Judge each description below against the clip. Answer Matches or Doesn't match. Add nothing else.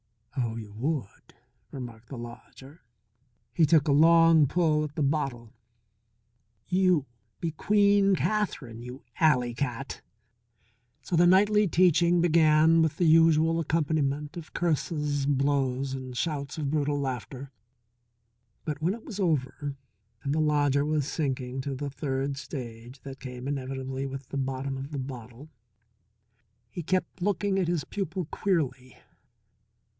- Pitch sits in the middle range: Matches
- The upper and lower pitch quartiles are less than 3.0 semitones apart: Doesn't match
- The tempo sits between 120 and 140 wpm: Matches